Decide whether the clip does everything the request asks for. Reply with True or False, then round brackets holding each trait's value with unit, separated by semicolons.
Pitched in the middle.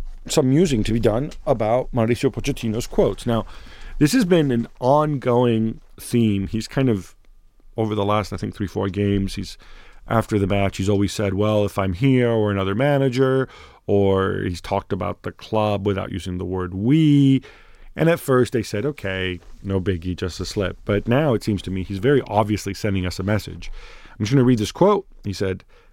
False (105 Hz)